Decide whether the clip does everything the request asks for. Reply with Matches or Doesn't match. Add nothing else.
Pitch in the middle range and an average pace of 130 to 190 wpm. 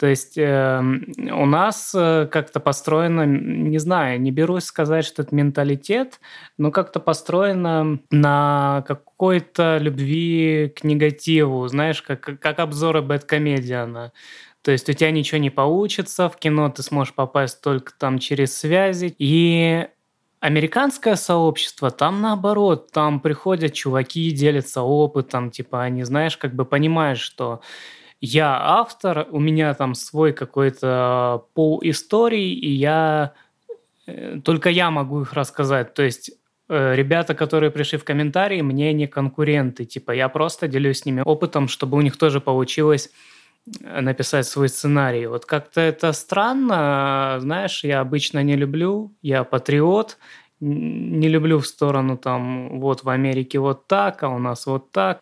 Matches